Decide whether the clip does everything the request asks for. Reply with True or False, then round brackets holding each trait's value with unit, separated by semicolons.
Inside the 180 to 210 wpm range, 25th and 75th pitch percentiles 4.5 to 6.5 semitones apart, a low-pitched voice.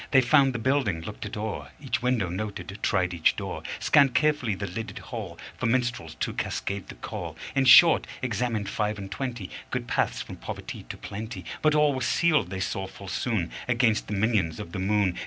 True (195 wpm; 5.0 semitones; 110 Hz)